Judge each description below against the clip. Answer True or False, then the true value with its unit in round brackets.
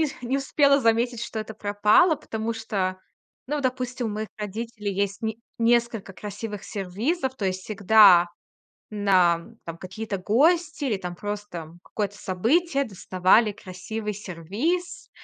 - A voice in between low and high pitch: False (215 Hz)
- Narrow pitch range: False (3.7 semitones)